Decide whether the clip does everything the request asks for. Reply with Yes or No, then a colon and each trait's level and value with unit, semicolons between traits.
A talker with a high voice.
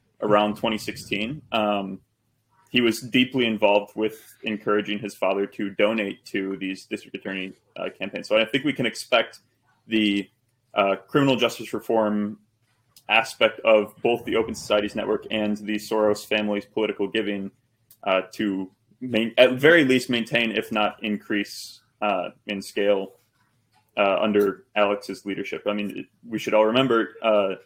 No: low, 110 Hz